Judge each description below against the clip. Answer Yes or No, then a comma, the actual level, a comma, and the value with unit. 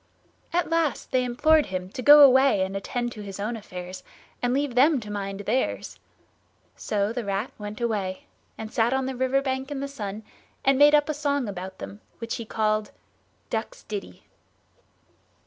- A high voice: Yes, high, 240 Hz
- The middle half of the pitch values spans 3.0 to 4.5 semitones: No, average, 5.1 semitones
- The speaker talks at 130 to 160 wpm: No, average, 180 wpm